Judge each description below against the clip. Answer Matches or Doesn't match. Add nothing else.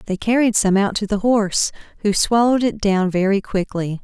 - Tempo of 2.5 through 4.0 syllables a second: Doesn't match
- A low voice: Doesn't match